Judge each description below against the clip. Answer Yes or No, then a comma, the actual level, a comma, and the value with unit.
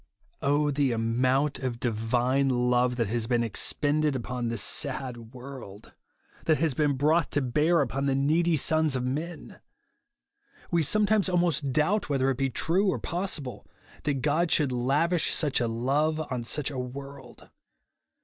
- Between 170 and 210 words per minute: No, average, 160 wpm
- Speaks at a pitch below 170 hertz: Yes, medium, 140 Hz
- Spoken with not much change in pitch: No, average, 3.7 semitones